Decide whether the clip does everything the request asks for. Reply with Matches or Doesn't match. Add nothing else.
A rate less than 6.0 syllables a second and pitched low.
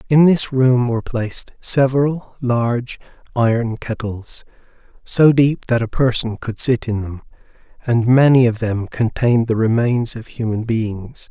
Matches